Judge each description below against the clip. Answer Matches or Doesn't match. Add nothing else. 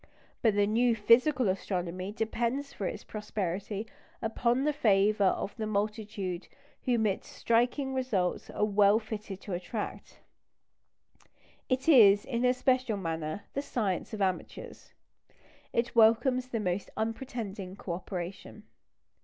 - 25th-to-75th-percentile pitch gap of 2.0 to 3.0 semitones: Doesn't match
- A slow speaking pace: Matches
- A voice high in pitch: Matches